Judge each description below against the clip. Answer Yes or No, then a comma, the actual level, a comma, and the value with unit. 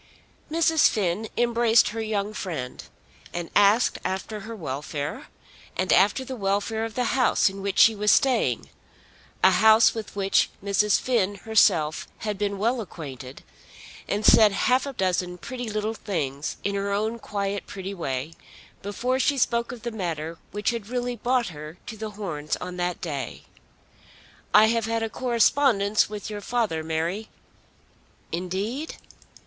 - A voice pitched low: No, high, 205 Hz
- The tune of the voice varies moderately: Yes, average, 4.0 semitones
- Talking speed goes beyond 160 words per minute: No, average, 155 wpm